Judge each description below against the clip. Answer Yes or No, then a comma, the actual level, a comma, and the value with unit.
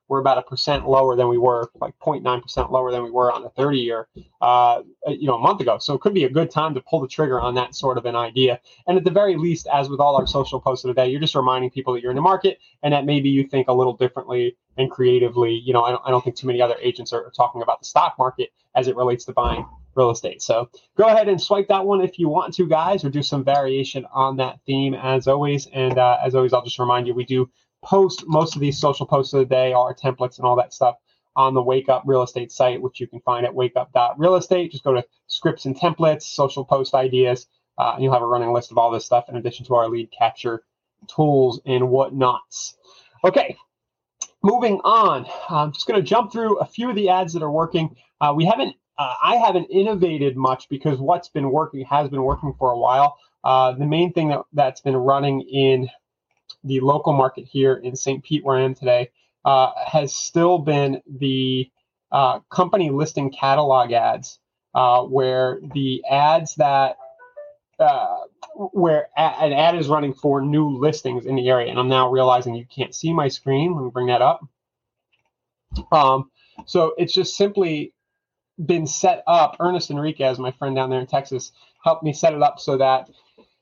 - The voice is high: No, low, 135 Hz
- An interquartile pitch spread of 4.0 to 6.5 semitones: No, average, 3.6 semitones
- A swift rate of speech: Yes, fast, 220 wpm